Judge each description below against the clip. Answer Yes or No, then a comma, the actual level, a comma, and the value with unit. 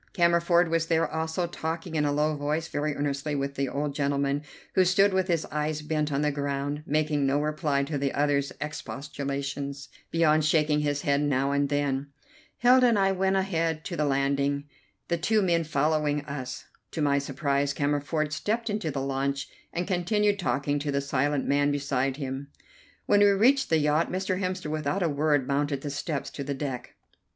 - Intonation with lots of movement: No, average, 2.9 semitones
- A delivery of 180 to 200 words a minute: Yes, average, 185 wpm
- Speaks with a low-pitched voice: No, medium, 150 Hz